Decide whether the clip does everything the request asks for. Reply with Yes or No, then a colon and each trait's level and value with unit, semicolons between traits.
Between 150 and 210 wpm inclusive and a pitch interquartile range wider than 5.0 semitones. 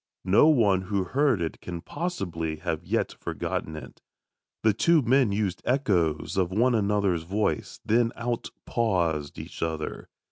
No: average, 140 wpm; wide, 5.6 semitones